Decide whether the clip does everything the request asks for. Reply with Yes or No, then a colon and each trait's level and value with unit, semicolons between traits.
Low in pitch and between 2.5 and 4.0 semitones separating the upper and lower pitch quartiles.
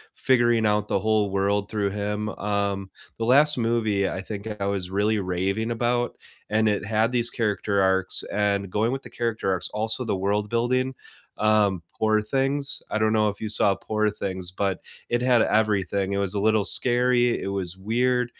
Yes: low, 105 Hz; average, 2.8 semitones